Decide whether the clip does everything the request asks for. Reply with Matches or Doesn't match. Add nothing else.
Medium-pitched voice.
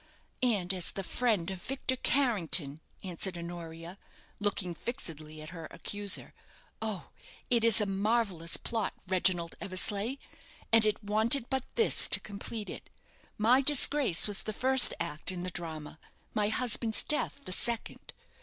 Doesn't match